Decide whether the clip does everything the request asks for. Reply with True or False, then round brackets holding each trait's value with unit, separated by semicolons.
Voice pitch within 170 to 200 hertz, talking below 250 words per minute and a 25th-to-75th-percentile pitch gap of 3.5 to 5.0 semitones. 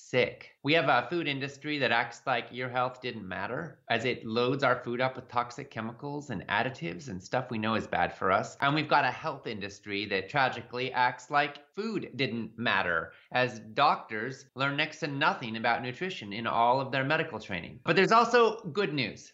False (125 Hz; 200 wpm; 3.8 semitones)